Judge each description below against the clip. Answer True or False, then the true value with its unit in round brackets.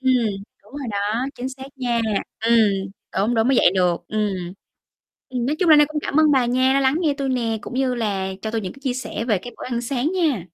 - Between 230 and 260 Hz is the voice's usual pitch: True (250 Hz)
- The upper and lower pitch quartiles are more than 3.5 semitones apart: False (3.2 semitones)